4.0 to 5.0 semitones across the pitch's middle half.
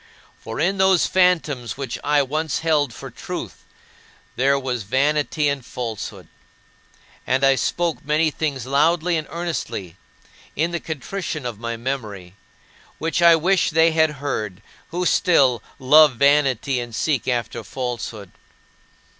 Yes: average, 4.6 semitones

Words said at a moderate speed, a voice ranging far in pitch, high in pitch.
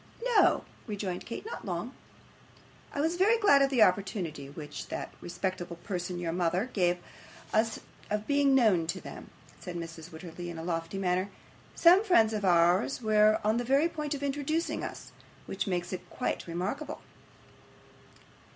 Yes: average, 160 wpm; wide, 7.8 semitones; high, 200 Hz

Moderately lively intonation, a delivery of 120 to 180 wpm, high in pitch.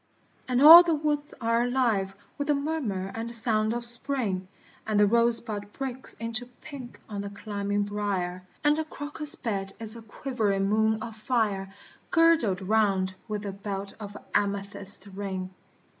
Yes: average, 3.9 semitones; average, 160 wpm; high, 220 Hz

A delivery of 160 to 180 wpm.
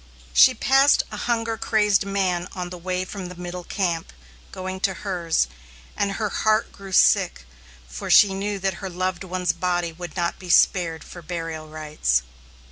Yes: average, 170 wpm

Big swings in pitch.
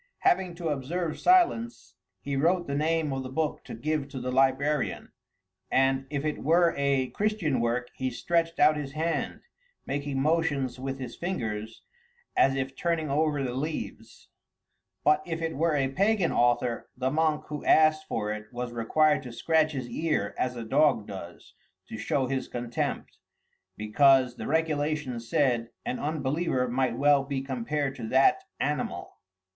No: average, 3.6 semitones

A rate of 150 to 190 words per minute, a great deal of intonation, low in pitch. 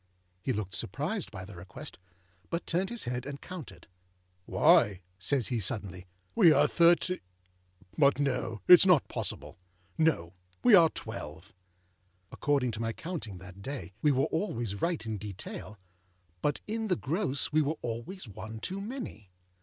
Yes: average, 155 wpm; wide, 8.2 semitones; low, 130 Hz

